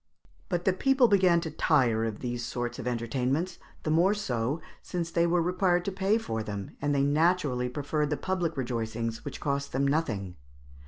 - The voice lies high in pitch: No, medium, 145 Hz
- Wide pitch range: Yes, wide, 6.4 semitones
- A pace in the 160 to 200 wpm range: Yes, average, 175 wpm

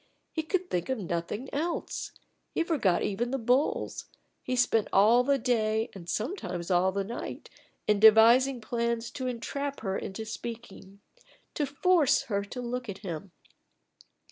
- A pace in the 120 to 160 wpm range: Yes, average, 150 wpm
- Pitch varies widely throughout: No, average, 4.7 semitones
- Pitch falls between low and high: No, high, 235 Hz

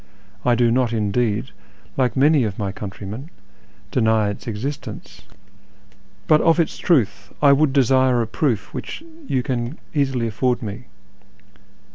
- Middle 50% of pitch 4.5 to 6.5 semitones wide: No, average, 3.9 semitones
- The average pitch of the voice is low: Yes, low, 125 Hz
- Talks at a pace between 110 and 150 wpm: Yes, average, 140 wpm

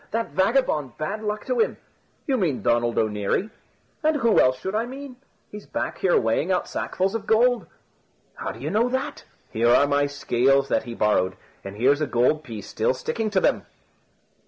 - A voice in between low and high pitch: Yes, medium, 155 Hz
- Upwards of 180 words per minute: Yes, average, 190 wpm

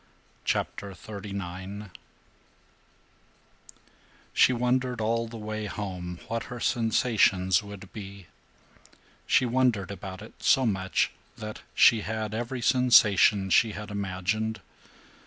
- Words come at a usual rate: No, slow, 105 wpm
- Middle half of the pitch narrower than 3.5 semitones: Yes, average, 2.9 semitones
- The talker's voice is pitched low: Yes, low, 105 Hz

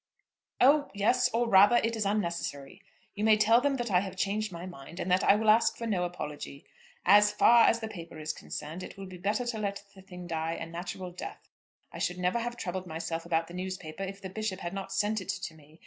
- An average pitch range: Yes, average, 3.8 semitones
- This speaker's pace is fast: Yes, fast, 235 wpm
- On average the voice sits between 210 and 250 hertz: No, high, 190 Hz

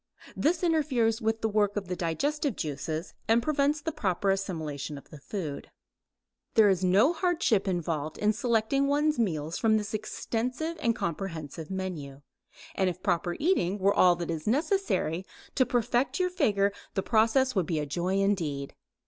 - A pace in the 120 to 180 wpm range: Yes, average, 165 wpm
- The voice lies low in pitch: No, high, 205 Hz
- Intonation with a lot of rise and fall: Yes, wide, 6.8 semitones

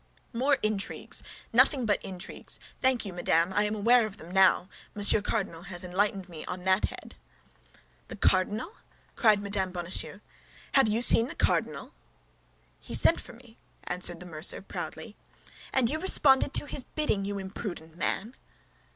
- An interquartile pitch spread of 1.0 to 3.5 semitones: No, average, 4.1 semitones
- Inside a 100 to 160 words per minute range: Yes, average, 155 wpm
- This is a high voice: Yes, high, 205 Hz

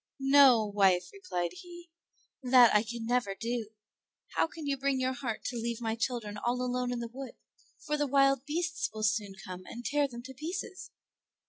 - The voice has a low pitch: No, very high, 250 Hz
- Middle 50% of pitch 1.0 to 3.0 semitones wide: No, average, 3.9 semitones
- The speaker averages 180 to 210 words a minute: Yes, average, 190 wpm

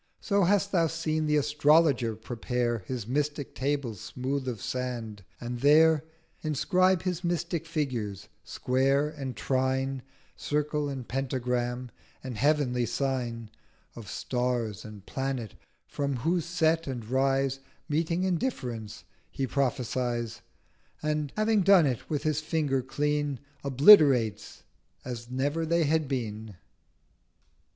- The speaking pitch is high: No, low, 135 Hz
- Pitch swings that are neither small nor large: Yes, average, 4.0 semitones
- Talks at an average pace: No, slow, 125 wpm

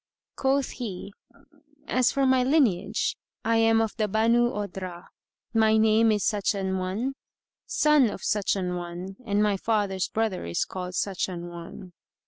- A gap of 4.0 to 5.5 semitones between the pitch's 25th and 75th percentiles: No, average, 3.4 semitones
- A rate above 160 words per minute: No, average, 155 wpm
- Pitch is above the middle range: Yes, high, 210 Hz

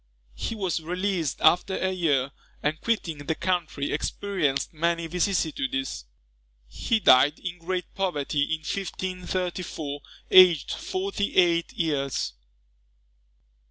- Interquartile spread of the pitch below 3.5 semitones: No, average, 4.1 semitones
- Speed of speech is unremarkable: No, slow, 105 wpm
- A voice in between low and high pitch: Yes, medium, 170 Hz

